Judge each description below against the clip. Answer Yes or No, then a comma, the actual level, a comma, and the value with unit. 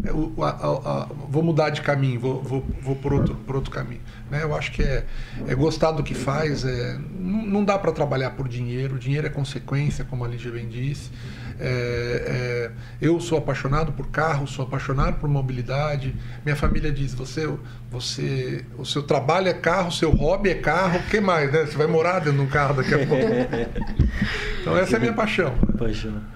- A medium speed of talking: Yes, average, 160 wpm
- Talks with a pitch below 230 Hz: Yes, medium, 140 Hz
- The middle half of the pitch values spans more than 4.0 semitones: No, average, 3.7 semitones